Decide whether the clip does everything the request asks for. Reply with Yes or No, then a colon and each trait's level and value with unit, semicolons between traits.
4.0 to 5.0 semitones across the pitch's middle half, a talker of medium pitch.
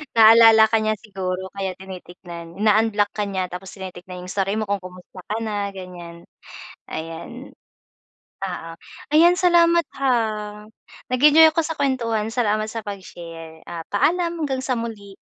No: average, 4.7 semitones; high, 205 Hz